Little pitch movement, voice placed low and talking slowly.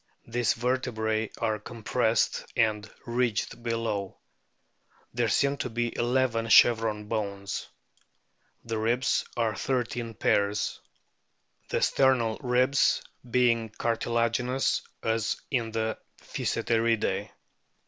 Yes: narrow, 1.8 semitones; low, 115 Hz; slow, 95 wpm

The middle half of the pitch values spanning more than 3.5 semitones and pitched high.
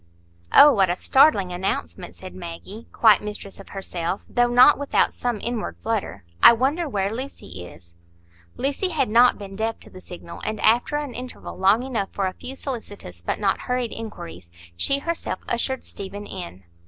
Yes: average, 4.9 semitones; high, 215 Hz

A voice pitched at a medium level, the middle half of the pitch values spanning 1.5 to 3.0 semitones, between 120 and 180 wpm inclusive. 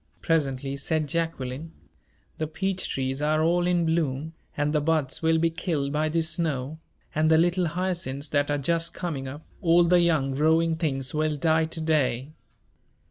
Yes: medium, 160 Hz; average, 2.7 semitones; average, 170 wpm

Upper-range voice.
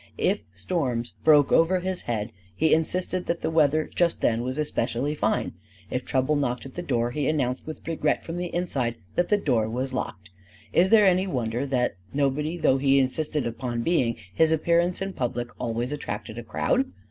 No: medium, 140 Hz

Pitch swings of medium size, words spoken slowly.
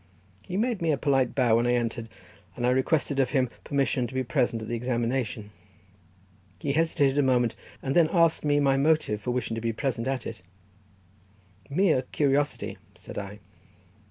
No: average, 3.6 semitones; average, 180 wpm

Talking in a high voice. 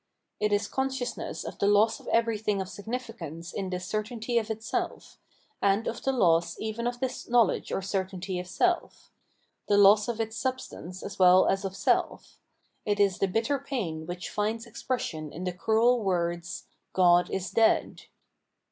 Yes: high, 205 Hz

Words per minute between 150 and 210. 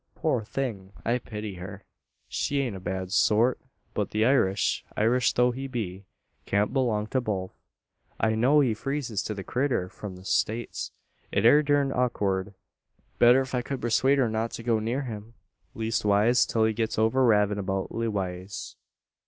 Yes: average, 170 wpm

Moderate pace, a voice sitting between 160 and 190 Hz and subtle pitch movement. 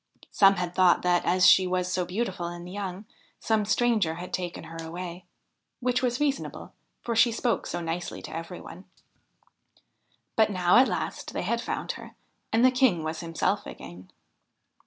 No: average, 170 wpm; medium, 185 Hz; average, 4.3 semitones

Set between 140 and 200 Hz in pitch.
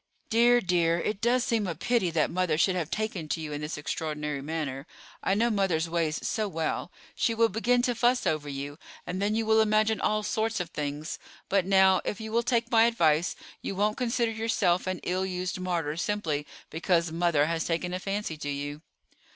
Yes: medium, 185 Hz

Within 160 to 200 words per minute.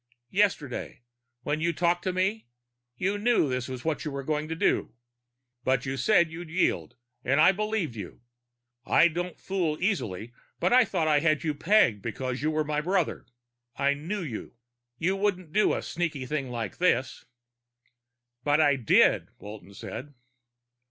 Yes: average, 165 wpm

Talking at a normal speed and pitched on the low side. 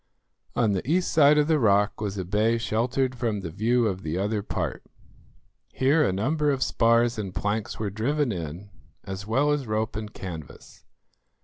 Yes: average, 180 wpm; low, 110 Hz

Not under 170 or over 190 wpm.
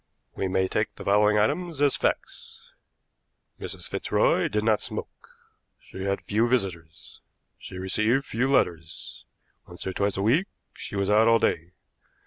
No: average, 150 wpm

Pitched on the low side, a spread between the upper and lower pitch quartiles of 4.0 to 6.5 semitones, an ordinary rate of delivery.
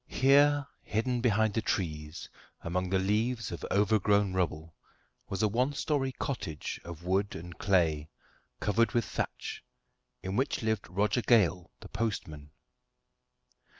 No: low, 100 Hz; average, 4.7 semitones; slow, 130 wpm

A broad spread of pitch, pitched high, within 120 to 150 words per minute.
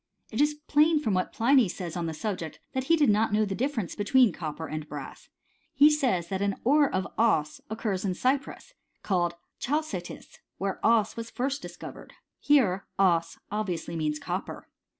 No: wide, 7.2 semitones; high, 210 Hz; average, 175 wpm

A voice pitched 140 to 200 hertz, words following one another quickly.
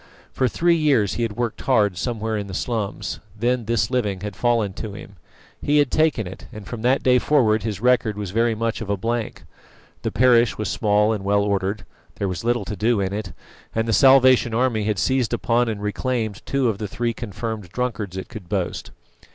No: low, 110 Hz; fast, 210 wpm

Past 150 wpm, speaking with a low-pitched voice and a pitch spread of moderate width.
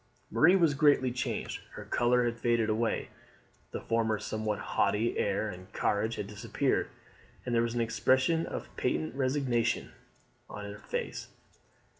No: average, 145 wpm; low, 115 Hz; average, 3.2 semitones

